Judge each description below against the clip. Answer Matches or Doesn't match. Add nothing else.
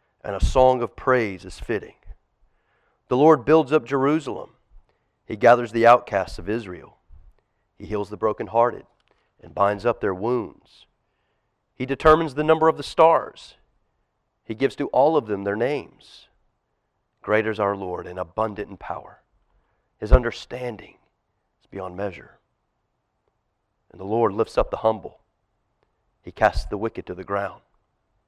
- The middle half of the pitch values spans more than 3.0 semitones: Matches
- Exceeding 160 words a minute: Doesn't match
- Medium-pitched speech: Doesn't match